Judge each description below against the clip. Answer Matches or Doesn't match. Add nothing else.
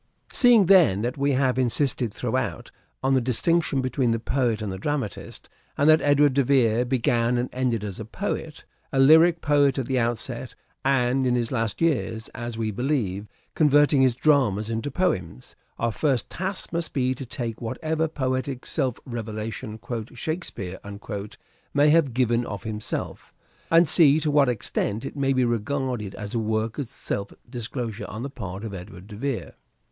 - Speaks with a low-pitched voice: Matches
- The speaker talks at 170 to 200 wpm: Matches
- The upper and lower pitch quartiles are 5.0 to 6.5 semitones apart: Doesn't match